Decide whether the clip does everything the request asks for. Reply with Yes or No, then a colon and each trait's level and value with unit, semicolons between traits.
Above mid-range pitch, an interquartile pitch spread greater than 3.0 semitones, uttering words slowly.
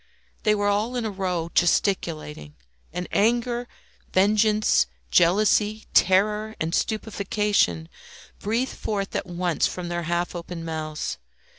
Yes: high, 195 Hz; average, 3.8 semitones; slow, 120 wpm